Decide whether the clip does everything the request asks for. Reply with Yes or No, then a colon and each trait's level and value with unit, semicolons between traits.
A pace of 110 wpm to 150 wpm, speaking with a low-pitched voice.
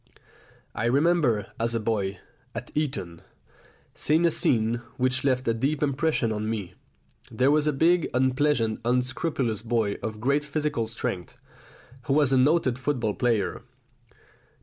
Yes: average, 140 wpm; low, 125 Hz